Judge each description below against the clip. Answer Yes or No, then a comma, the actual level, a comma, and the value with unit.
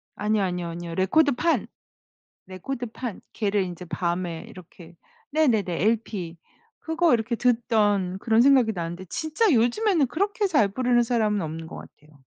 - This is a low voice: No, high, 215 Hz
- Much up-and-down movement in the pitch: Yes, wide, 5.9 semitones